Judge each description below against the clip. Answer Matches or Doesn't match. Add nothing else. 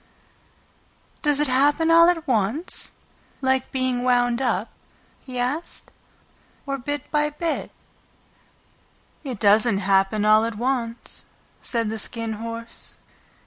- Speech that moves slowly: Matches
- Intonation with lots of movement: Doesn't match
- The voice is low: Doesn't match